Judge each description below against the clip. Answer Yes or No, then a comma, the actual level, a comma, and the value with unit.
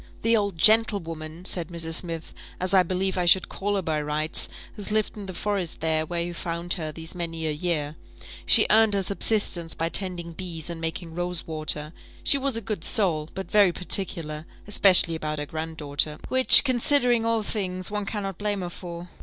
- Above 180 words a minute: Yes, average, 195 wpm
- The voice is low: No, medium, 175 Hz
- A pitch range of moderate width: Yes, average, 3.8 semitones